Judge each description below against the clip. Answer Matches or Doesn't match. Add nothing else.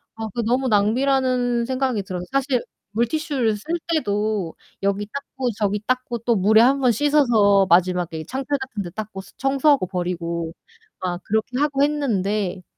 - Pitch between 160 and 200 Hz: Doesn't match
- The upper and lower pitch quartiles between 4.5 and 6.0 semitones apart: Matches